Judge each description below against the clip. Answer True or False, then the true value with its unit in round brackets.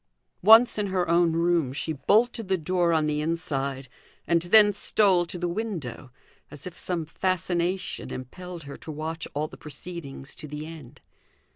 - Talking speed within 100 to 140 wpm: False (165 wpm)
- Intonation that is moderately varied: True (3.4 semitones)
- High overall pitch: False (170 Hz)